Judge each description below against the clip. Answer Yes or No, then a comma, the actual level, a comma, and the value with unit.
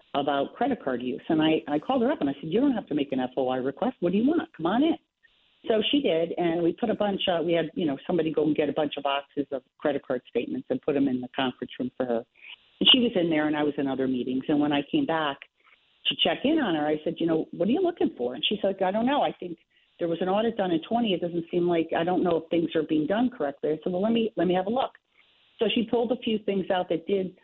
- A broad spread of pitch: Yes, wide, 6.8 semitones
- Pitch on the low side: No, medium, 170 Hz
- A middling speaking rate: No, fast, 300 wpm